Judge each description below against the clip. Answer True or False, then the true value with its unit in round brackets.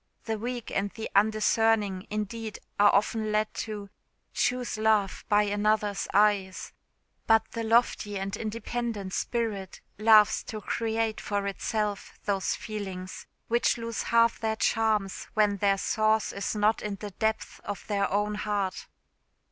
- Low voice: False (210 Hz)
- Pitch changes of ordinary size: False (1.7 semitones)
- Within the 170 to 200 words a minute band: False (140 wpm)